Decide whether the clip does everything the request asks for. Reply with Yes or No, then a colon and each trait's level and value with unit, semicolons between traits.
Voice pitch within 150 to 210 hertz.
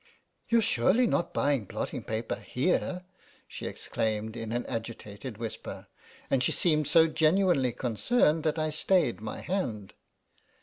No: low, 135 Hz